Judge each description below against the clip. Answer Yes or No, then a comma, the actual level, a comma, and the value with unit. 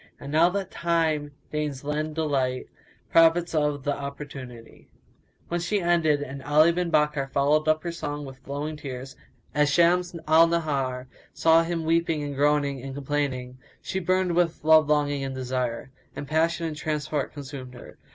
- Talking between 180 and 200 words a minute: No, average, 165 wpm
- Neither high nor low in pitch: Yes, medium, 150 Hz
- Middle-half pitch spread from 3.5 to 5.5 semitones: No, average, 2.9 semitones